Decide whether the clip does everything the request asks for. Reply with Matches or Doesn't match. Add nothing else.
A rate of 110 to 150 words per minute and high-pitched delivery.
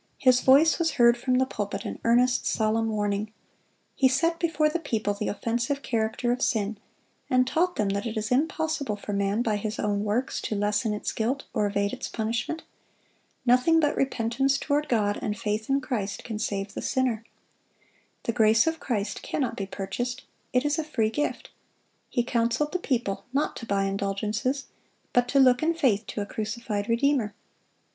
Doesn't match